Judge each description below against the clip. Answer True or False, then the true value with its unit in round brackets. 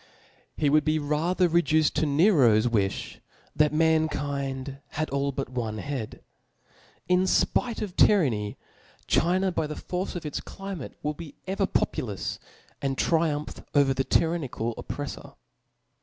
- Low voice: False (150 Hz)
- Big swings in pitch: False (4.1 semitones)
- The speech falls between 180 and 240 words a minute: False (135 wpm)